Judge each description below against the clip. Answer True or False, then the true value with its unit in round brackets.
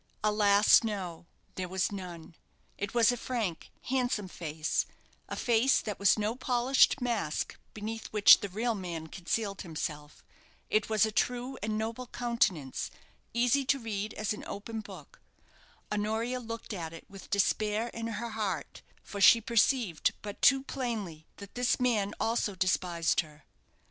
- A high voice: True (215 Hz)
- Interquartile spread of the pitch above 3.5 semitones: True (3.9 semitones)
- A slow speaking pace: False (150 wpm)